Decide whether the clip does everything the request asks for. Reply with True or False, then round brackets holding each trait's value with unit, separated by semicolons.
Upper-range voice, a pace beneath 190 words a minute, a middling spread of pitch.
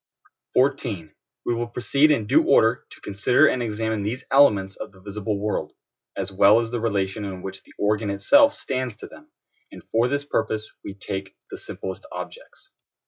False (110 Hz; 180 wpm; 4.2 semitones)